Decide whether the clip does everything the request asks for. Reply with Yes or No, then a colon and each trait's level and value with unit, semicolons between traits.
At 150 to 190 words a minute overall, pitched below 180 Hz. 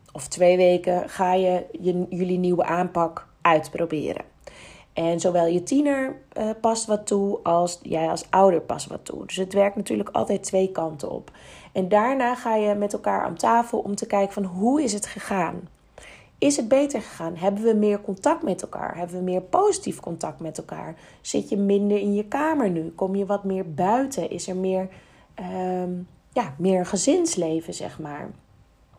No: average, 180 wpm; high, 195 Hz